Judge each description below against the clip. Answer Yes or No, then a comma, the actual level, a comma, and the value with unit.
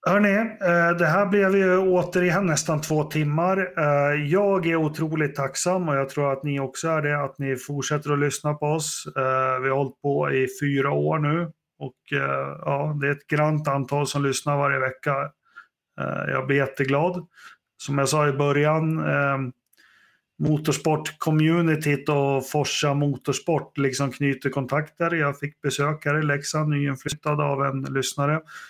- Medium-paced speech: Yes, average, 155 wpm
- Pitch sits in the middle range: Yes, medium, 145 Hz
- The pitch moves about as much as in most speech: No, narrow, 2.3 semitones